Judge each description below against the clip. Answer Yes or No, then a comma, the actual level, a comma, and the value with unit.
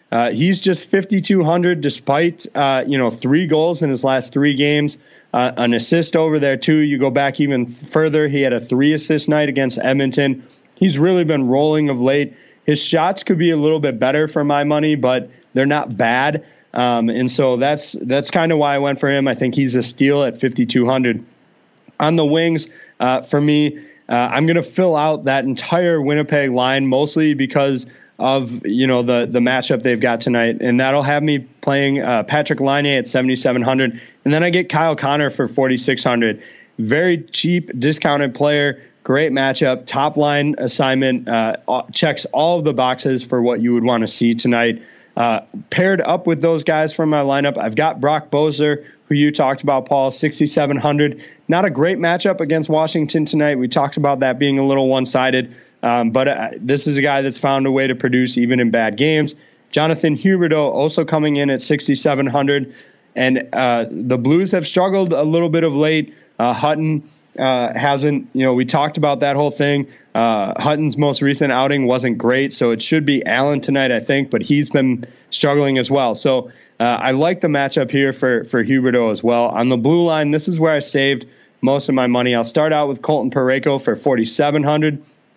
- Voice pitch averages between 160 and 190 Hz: No, medium, 140 Hz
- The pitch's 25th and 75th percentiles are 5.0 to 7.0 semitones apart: No, average, 2.9 semitones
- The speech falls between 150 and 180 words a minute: No, average, 195 wpm